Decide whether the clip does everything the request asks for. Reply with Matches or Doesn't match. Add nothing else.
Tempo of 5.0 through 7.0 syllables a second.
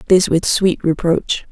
Doesn't match